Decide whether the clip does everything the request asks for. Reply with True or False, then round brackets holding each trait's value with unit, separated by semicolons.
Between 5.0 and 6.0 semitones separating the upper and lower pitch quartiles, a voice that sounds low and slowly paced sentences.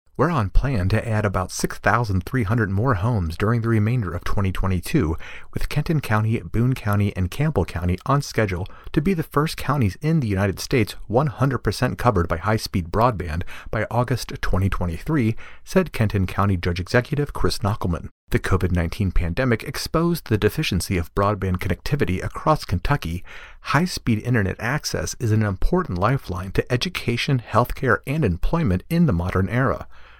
False (5.3 semitones; 105 Hz; 150 wpm)